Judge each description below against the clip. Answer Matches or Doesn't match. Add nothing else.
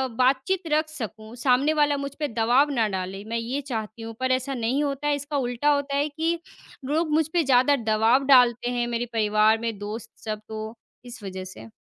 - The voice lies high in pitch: Matches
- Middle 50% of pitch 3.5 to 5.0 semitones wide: Matches